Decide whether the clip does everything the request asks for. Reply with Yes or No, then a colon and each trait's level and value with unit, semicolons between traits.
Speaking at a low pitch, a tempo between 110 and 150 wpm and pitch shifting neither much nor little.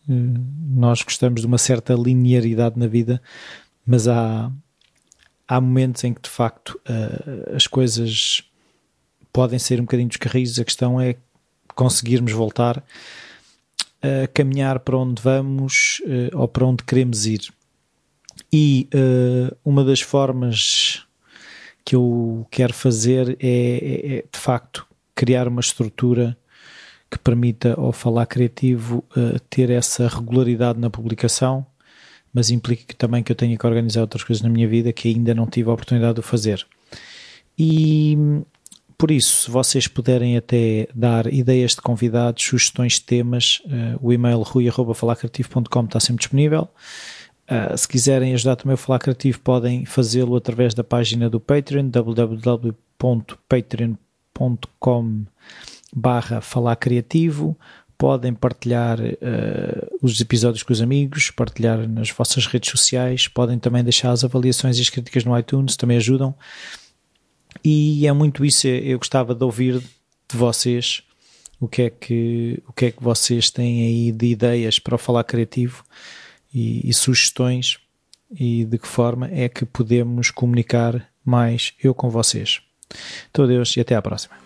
No: low, 125 Hz; average, 145 wpm; narrow, 1.5 semitones